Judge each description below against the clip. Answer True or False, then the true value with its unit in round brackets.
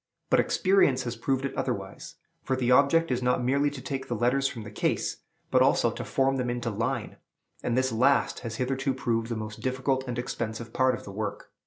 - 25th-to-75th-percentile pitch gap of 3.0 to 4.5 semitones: False (2.4 semitones)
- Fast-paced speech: True (210 wpm)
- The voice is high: False (125 Hz)